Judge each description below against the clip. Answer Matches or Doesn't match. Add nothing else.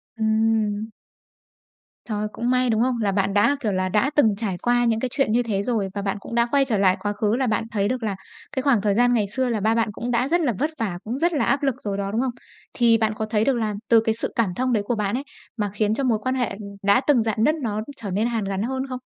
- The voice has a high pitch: Matches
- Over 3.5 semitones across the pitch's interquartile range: Doesn't match